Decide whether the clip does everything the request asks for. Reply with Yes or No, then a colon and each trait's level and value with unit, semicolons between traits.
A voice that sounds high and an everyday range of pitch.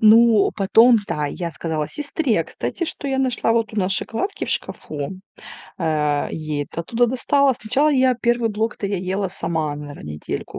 No: high, 210 Hz; wide, 7.1 semitones